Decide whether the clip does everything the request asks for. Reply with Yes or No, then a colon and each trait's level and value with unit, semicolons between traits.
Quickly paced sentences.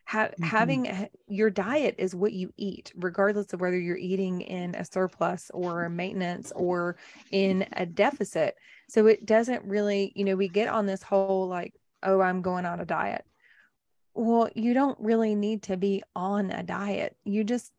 No: average, 180 wpm